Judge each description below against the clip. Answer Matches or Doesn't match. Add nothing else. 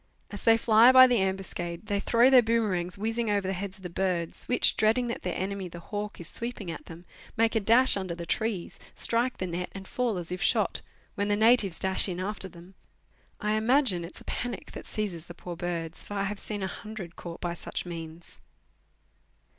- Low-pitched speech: Doesn't match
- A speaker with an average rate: Doesn't match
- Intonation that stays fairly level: Doesn't match